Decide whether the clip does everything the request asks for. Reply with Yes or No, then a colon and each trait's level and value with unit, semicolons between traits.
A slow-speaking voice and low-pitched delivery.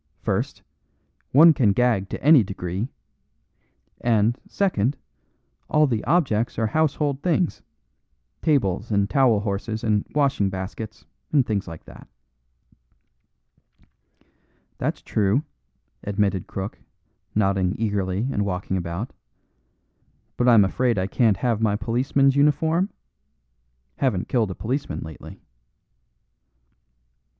Yes: slow, 105 wpm; low, 110 Hz